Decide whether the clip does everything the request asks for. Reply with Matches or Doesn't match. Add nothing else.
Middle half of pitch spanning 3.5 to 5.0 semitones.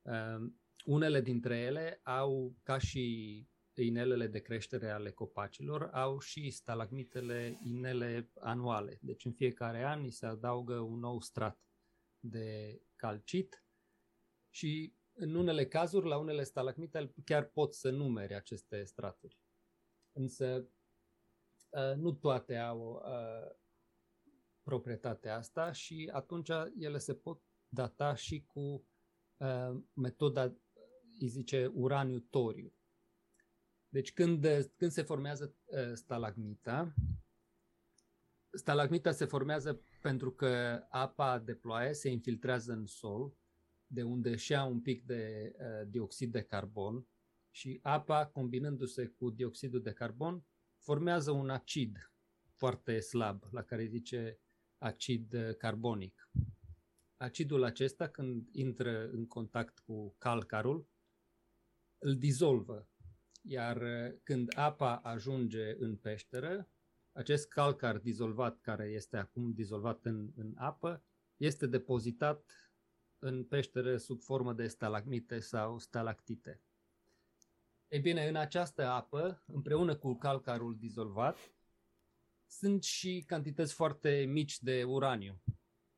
Matches